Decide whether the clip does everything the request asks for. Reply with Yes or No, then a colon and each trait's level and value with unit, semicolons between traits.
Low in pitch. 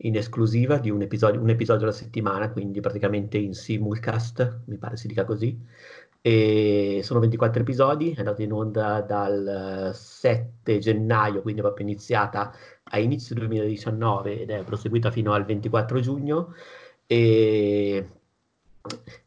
Yes: low, 110 Hz